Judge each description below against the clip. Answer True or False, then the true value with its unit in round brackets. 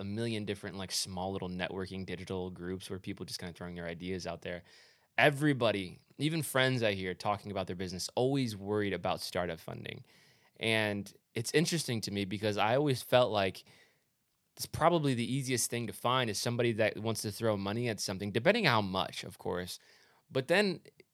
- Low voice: True (105 Hz)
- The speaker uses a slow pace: False (185 wpm)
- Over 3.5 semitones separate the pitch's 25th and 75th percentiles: True (4.3 semitones)